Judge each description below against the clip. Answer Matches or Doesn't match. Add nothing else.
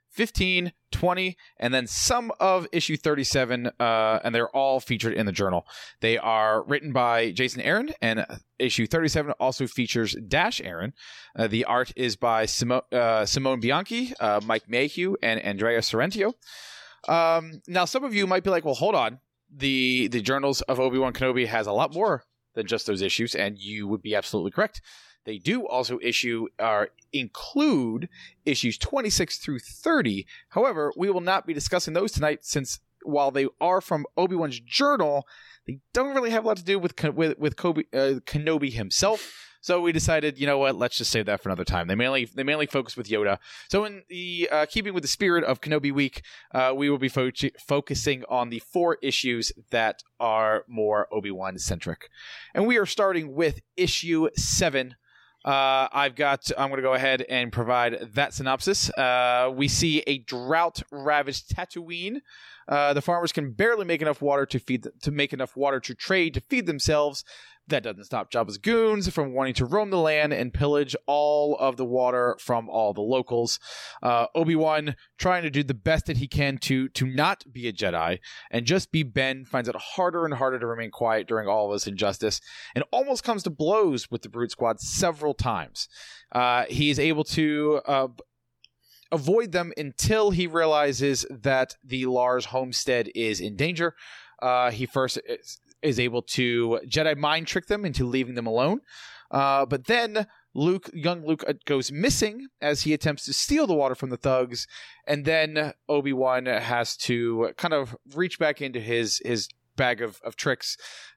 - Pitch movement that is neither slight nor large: Matches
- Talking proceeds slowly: Doesn't match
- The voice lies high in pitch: Doesn't match